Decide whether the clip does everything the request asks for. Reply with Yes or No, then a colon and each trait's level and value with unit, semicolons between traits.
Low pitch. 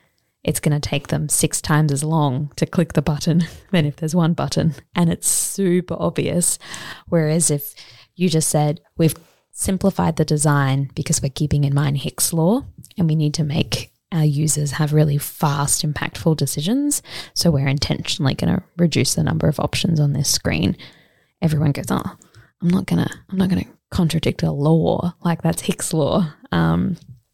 No: medium, 155 Hz